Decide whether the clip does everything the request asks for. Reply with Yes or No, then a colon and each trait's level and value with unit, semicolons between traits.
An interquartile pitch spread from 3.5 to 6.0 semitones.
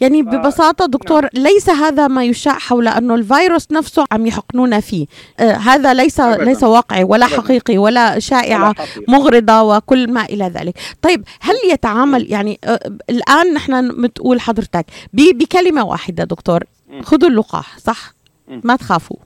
Yes: average, 4.7 semitones